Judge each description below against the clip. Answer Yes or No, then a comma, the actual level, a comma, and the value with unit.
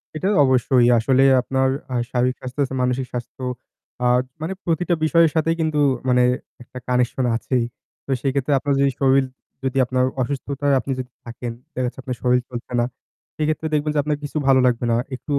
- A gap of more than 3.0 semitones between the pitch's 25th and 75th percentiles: No, narrow, 2.6 semitones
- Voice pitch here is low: Yes, low, 130 Hz